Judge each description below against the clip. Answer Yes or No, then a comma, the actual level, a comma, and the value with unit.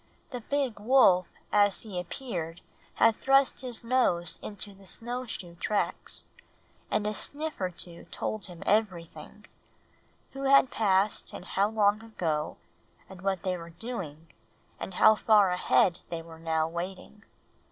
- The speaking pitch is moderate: No, high, 200 Hz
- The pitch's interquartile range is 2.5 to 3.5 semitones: No, average, 4.7 semitones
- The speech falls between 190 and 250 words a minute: No, average, 145 wpm